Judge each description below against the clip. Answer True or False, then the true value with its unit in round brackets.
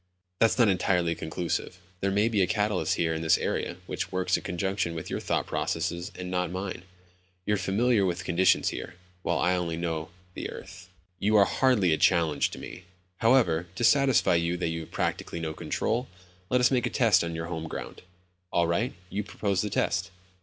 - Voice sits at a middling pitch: False (90 Hz)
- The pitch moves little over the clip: False (3.4 semitones)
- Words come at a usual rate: True (195 wpm)